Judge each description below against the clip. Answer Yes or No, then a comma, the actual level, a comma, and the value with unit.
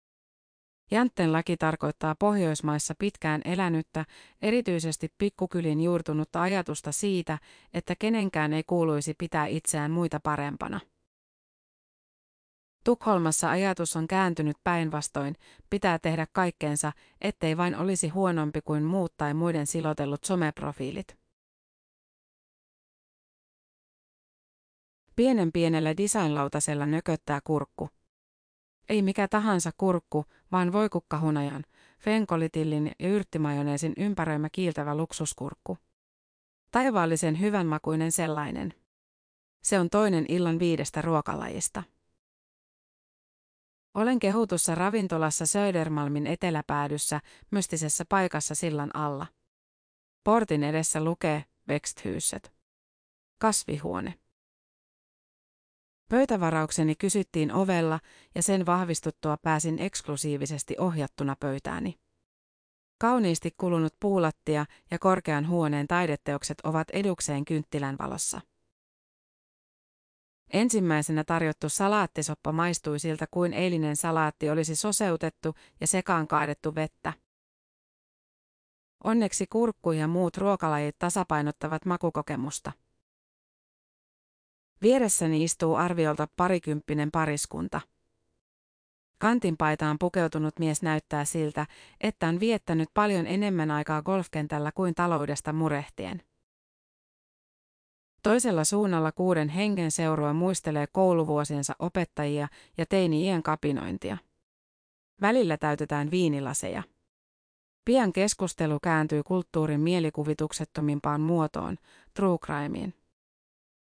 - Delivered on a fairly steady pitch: No, average, 3.3 semitones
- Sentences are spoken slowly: Yes, slow, 85 wpm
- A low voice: No, medium, 160 Hz